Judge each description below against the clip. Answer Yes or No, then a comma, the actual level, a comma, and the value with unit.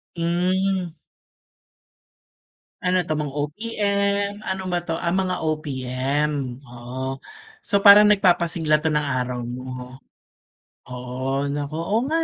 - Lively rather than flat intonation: Yes, wide, 6.1 semitones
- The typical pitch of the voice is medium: Yes, medium, 155 Hz